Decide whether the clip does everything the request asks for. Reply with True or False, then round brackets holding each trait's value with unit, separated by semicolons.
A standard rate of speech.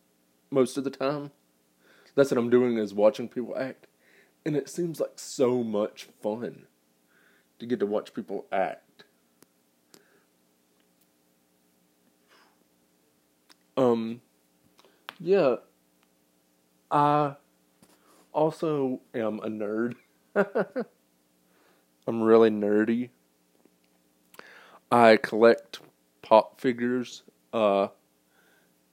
False (85 wpm)